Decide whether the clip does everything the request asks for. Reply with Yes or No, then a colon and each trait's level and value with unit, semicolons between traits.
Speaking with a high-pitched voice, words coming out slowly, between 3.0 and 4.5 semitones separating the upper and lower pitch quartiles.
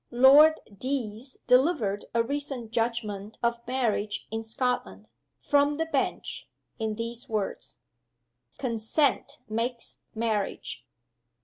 Yes: high, 235 Hz; slow, 100 wpm; average, 3.5 semitones